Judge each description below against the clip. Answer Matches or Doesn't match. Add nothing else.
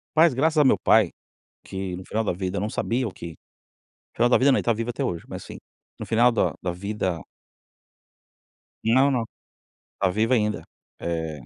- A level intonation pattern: Doesn't match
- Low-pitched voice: Matches